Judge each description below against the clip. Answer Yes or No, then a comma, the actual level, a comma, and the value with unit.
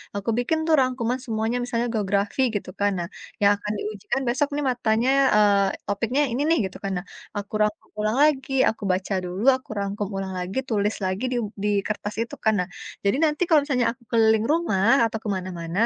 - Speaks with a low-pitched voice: No, high, 215 Hz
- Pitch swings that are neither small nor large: Yes, average, 3.7 semitones